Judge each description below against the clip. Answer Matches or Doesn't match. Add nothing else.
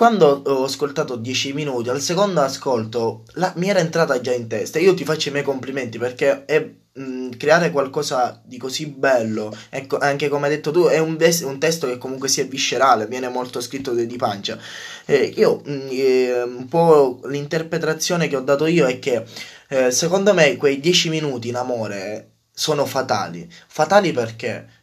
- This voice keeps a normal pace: Doesn't match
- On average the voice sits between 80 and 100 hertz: Doesn't match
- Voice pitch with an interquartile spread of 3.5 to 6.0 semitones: Matches